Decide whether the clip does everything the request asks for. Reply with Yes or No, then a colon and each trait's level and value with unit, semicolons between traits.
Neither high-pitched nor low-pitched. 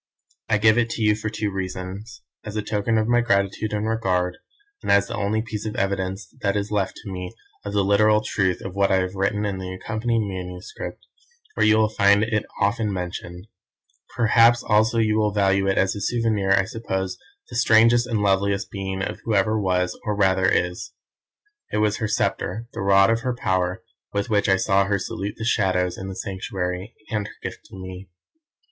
No: low, 100 Hz